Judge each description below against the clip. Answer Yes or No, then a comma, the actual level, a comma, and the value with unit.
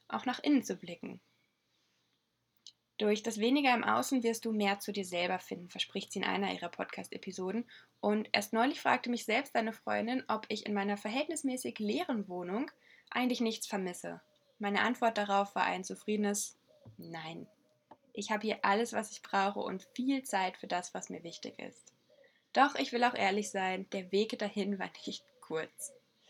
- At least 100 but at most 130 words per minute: No, average, 175 wpm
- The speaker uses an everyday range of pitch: Yes, average, 3.5 semitones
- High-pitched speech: Yes, high, 215 Hz